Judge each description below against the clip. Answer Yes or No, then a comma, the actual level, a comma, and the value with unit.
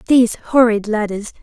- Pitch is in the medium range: No, high, 225 Hz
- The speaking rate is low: Yes, slow, 125 wpm